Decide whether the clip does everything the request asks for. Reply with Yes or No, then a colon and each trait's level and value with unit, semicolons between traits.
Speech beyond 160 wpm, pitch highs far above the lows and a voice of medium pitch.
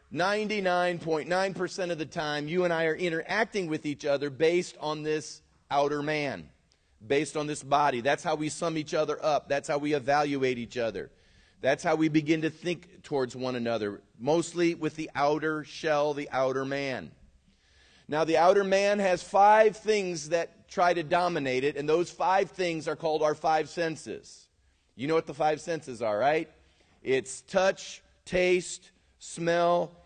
No: average, 170 wpm; average, 3.6 semitones; medium, 155 Hz